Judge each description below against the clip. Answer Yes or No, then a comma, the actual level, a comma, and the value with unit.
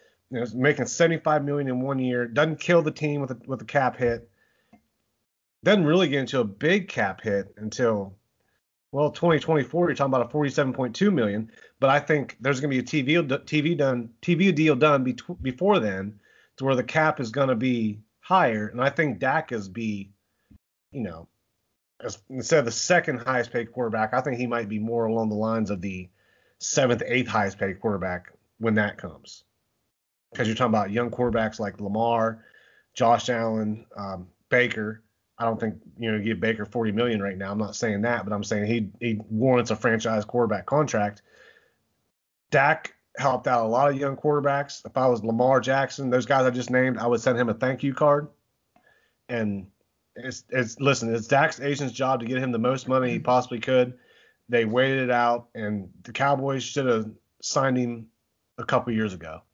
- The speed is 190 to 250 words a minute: Yes, average, 200 wpm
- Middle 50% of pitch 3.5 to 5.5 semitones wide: Yes, average, 4.0 semitones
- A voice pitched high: No, low, 120 Hz